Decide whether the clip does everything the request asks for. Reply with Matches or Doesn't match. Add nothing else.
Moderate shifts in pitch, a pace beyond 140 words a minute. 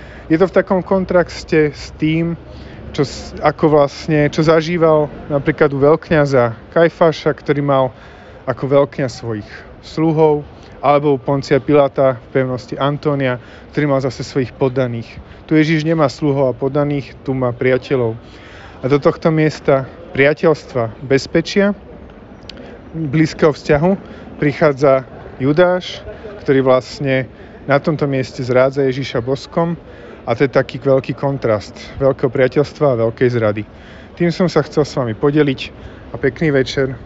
Doesn't match